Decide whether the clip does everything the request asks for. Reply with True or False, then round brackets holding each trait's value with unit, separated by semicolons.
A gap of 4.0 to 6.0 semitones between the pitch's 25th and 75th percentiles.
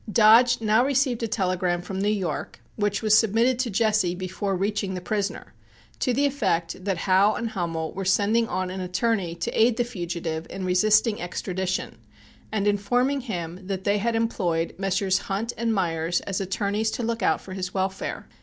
False (3.5 semitones)